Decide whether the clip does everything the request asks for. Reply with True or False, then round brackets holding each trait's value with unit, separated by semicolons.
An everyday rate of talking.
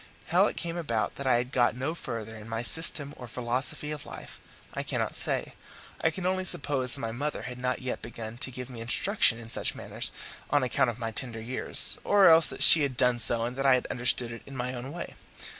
False (235 wpm)